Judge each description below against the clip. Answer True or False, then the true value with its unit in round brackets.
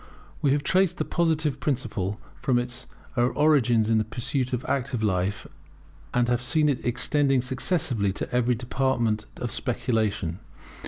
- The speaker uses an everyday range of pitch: True (3.7 semitones)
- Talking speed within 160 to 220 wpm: False (145 wpm)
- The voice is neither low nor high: False (125 Hz)